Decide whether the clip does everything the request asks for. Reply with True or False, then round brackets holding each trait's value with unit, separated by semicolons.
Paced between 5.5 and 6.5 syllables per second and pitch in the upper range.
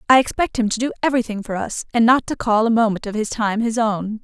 True (6.2 syllables/s; 225 Hz)